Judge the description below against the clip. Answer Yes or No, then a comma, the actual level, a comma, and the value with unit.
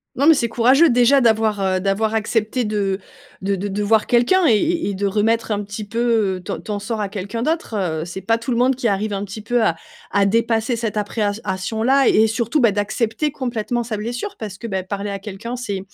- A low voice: No, high, 220 Hz